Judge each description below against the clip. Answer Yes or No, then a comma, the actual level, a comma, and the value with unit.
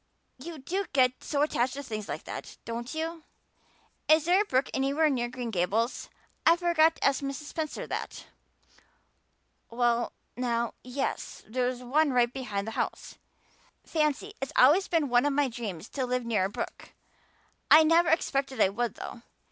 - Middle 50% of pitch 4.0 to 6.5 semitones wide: Yes, average, 4.5 semitones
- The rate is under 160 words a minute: No, average, 165 wpm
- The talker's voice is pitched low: No, very high, 260 Hz